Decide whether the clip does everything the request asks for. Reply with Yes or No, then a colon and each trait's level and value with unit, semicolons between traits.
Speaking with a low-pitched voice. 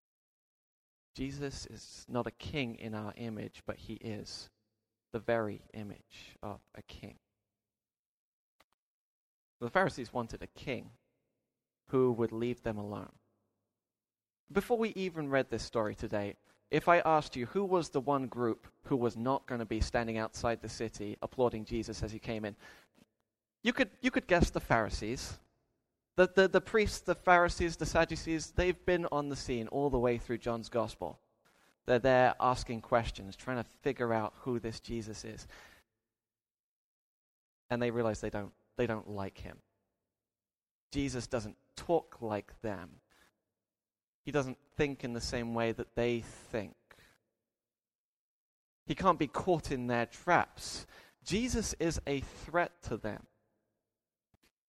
Yes: low, 115 Hz